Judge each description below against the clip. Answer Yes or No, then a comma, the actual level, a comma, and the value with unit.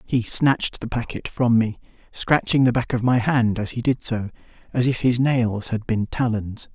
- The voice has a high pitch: No, low, 120 Hz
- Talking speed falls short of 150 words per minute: No, fast, 205 wpm